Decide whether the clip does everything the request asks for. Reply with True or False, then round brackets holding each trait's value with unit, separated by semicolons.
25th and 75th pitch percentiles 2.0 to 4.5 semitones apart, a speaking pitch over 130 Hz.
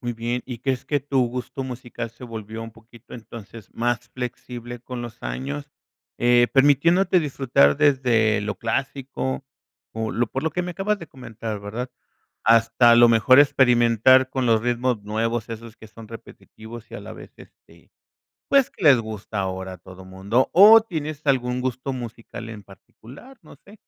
False (2.9 semitones; 120 Hz)